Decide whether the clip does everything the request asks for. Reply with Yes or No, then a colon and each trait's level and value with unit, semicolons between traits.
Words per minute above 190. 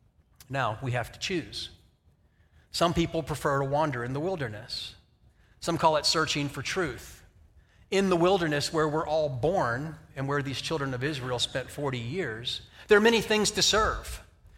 No: average, 170 wpm